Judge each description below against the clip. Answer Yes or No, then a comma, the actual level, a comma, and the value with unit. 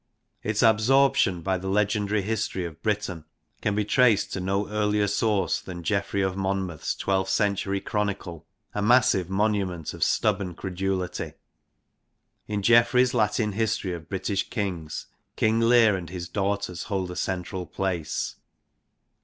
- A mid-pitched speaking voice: No, low, 100 Hz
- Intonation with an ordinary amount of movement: No, narrow, 2.3 semitones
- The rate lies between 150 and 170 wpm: No, slow, 135 wpm